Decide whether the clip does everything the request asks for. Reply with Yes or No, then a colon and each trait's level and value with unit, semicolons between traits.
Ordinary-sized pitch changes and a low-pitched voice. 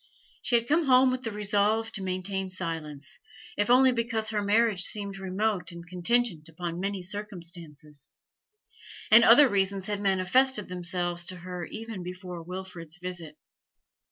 No: average, 3.7 semitones; high, 190 Hz